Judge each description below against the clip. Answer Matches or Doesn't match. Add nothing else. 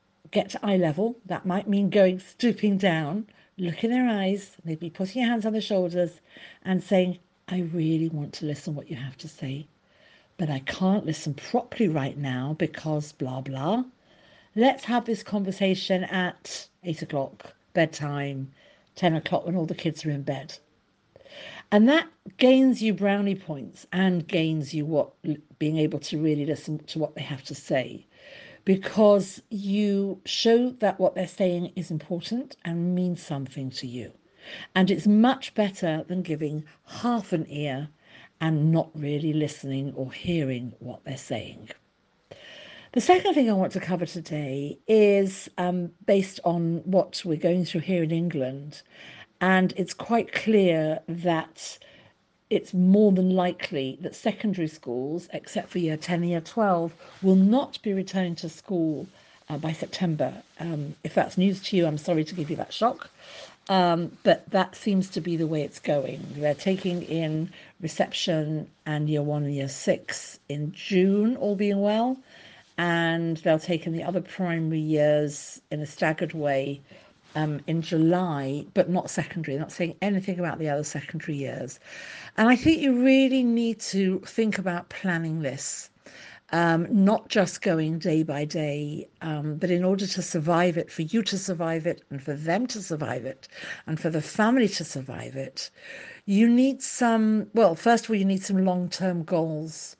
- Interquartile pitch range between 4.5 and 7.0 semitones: Doesn't match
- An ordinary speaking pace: Matches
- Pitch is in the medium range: Matches